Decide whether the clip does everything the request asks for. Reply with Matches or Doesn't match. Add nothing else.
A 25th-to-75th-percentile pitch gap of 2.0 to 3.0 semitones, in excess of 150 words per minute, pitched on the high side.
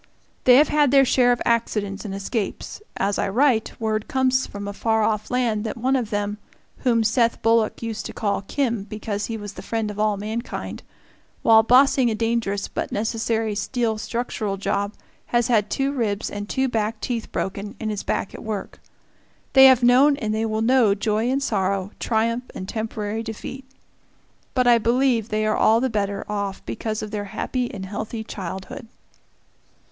Matches